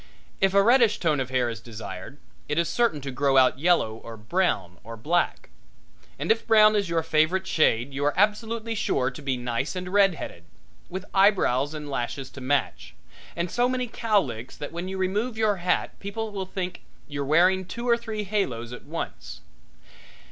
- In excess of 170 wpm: Yes, average, 185 wpm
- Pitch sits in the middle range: Yes, medium, 170 Hz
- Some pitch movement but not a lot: No, wide, 7.4 semitones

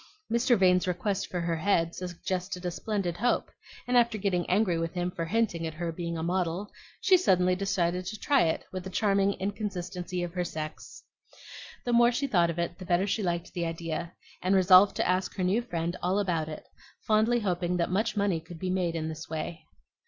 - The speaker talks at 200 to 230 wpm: Yes, fast, 205 wpm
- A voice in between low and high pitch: Yes, medium, 180 Hz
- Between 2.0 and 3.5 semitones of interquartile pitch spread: Yes, average, 2.8 semitones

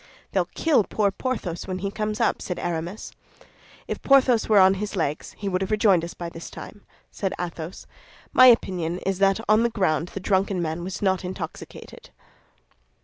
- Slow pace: No, average, 180 wpm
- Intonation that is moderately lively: Yes, average, 3.3 semitones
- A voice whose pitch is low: No, high, 190 Hz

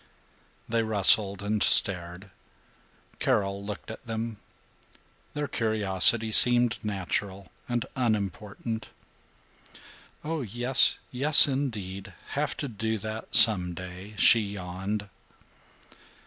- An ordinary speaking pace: No, slow, 95 wpm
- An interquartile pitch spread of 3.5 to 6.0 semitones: No, average, 3.0 semitones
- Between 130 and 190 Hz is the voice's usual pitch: No, low, 105 Hz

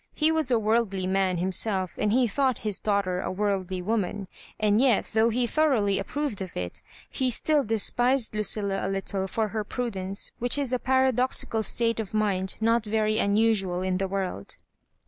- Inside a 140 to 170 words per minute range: No, average, 180 wpm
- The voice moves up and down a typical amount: Yes, average, 3.6 semitones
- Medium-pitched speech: No, high, 215 Hz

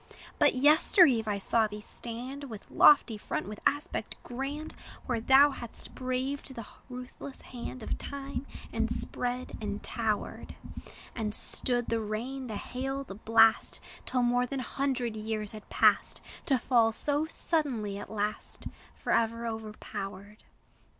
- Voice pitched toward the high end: Yes, high, 240 Hz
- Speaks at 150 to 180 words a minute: No, average, 140 wpm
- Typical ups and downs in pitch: Yes, average, 3.7 semitones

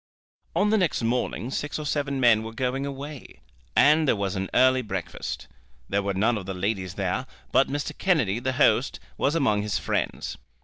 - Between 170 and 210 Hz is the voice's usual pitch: No, low, 125 Hz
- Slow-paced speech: No, average, 185 wpm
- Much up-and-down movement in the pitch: Yes, wide, 5.8 semitones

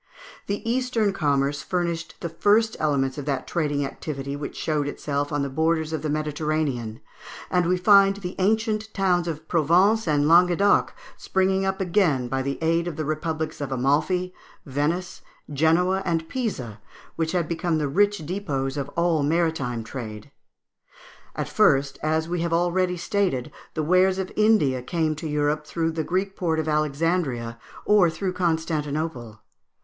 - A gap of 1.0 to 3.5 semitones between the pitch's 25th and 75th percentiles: No, average, 4.0 semitones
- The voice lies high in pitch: No, medium, 160 Hz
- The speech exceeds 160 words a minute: No, average, 155 wpm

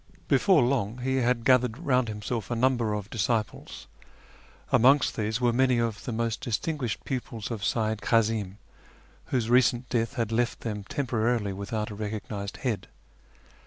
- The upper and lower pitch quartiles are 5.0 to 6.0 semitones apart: No, narrow, 2.6 semitones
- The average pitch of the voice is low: Yes, low, 115 Hz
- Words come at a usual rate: Yes, average, 150 wpm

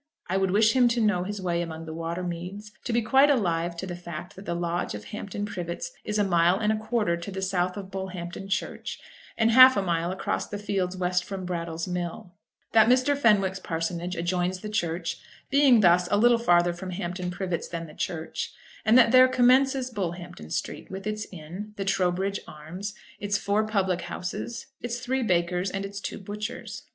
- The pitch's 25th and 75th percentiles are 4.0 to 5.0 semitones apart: No, average, 3.5 semitones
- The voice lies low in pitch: No, high, 190 Hz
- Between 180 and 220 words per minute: Yes, average, 200 wpm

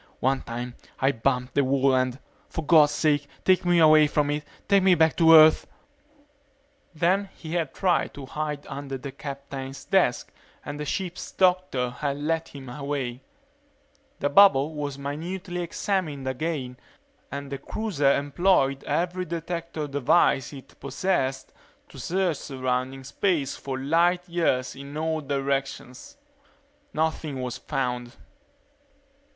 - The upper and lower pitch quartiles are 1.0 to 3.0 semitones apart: No, average, 4.0 semitones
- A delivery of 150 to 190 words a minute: No, slow, 135 wpm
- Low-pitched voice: No, medium, 145 Hz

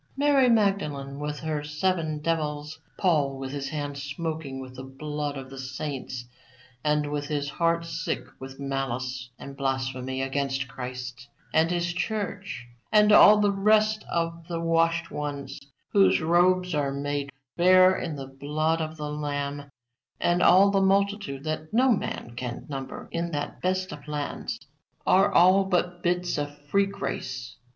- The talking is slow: No, average, 155 wpm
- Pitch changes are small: No, average, 4.5 semitones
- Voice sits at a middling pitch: Yes, medium, 150 Hz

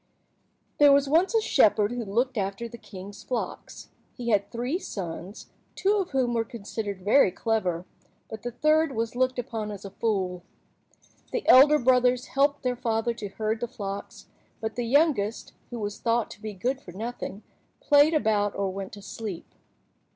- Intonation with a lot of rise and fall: No, average, 4.0 semitones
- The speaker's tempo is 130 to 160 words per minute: No, average, 175 wpm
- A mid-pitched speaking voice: No, high, 230 Hz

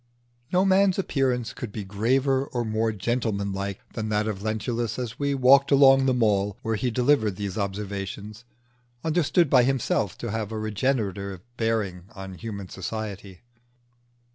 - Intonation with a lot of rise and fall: No, average, 4.5 semitones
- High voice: No, low, 110 Hz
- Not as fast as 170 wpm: Yes, average, 150 wpm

